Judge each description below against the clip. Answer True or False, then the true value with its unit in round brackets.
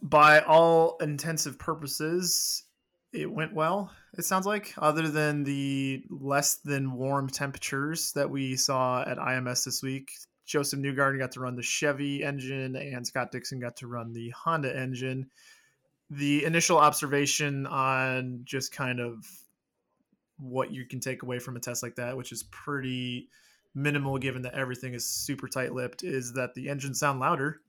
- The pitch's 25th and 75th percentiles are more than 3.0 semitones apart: False (2.7 semitones)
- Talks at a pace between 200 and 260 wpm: False (165 wpm)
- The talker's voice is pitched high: False (135 Hz)